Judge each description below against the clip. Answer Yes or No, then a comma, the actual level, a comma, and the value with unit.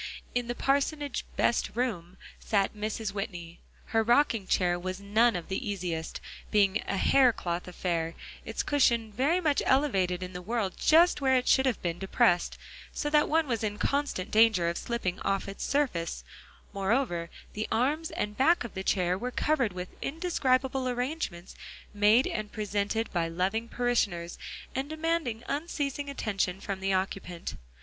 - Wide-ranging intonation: Yes, wide, 6.0 semitones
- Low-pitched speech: No, high, 220 Hz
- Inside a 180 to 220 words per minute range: No, average, 160 wpm